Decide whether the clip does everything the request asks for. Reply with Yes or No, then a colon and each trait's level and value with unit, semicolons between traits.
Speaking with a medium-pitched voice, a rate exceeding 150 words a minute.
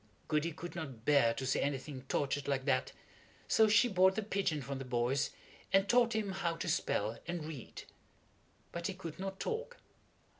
Yes: medium, 160 Hz; average, 180 wpm